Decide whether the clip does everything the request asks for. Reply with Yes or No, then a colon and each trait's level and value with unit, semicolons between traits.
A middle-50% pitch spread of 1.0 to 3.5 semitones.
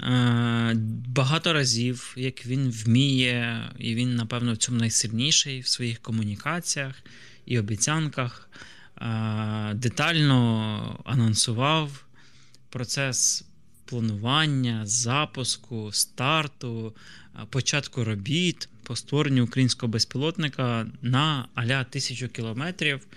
Yes: average, 3.0 semitones